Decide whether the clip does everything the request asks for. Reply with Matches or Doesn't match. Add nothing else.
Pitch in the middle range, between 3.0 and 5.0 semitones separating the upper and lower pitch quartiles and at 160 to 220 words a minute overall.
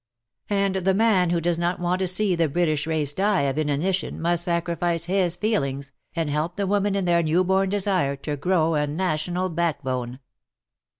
Matches